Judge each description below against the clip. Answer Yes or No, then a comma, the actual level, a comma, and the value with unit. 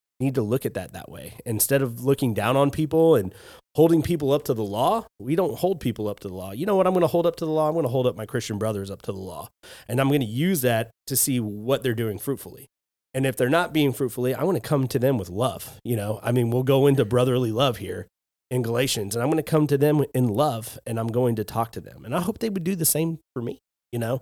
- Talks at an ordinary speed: No, fast, 290 wpm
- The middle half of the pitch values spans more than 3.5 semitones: Yes, average, 4.4 semitones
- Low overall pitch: Yes, low, 130 Hz